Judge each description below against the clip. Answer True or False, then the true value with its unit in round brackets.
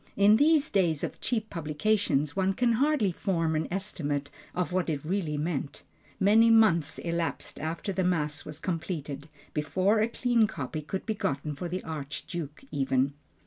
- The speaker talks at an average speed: True (160 wpm)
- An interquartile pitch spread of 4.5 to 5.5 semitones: True (5.2 semitones)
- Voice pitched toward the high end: False (170 Hz)